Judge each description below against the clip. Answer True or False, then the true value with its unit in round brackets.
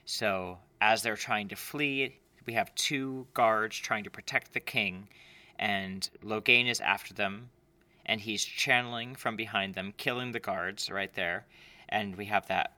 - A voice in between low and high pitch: False (110 Hz)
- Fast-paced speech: False (165 wpm)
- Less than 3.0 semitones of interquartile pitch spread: False (3.8 semitones)